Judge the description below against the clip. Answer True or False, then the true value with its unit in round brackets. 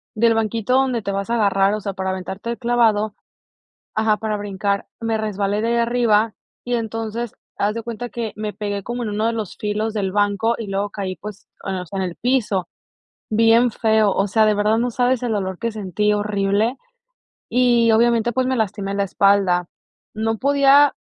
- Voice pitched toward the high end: True (215 Hz)